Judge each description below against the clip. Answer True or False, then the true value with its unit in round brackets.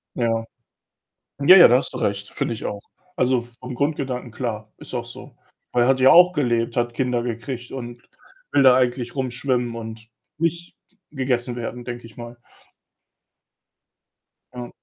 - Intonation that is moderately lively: False (1.8 semitones)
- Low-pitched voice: True (120 Hz)